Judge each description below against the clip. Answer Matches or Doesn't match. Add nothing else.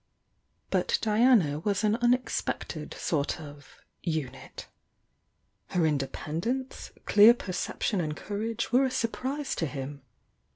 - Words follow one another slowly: Matches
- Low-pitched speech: Doesn't match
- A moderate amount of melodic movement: Doesn't match